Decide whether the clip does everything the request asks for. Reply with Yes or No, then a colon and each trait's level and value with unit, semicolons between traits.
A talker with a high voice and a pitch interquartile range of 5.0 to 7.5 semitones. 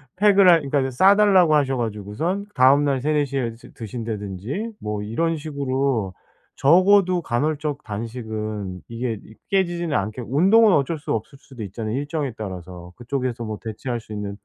No: low, 130 Hz; wide, 6.3 semitones